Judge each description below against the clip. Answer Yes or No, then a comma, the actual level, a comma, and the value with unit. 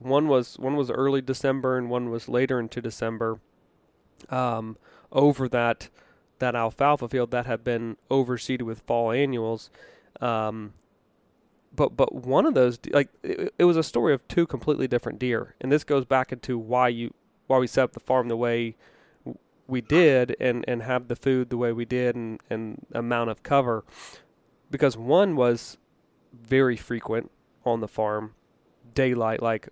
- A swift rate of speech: No, average, 170 wpm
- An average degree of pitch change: No, narrow, 2.3 semitones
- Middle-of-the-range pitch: No, low, 125 Hz